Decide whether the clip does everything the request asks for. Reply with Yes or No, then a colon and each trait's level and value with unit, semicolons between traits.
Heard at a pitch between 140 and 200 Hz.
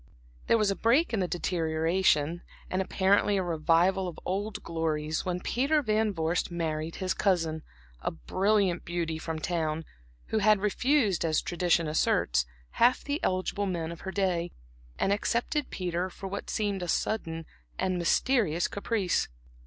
Yes: medium, 185 Hz